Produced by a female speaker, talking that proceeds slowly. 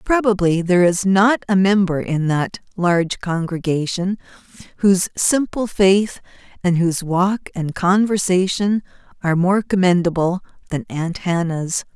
Yes: female; slow, 120 wpm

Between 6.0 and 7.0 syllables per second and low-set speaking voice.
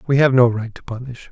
Yes: 6.1 syllables/s; low, 125 Hz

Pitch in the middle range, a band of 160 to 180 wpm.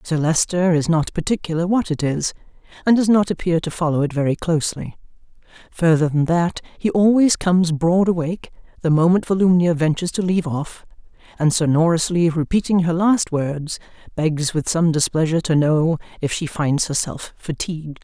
Yes: medium, 165 Hz; average, 165 wpm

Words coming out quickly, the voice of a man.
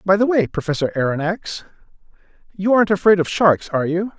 No: average, 170 wpm; male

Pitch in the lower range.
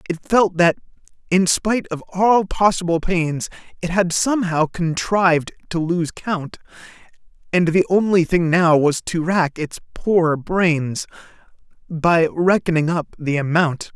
No: medium, 170 Hz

